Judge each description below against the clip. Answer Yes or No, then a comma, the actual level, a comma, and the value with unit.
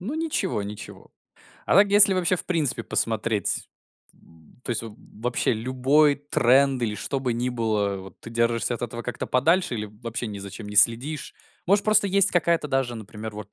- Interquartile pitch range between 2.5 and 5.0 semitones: No, wide, 5.6 semitones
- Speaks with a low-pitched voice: Yes, low, 120 Hz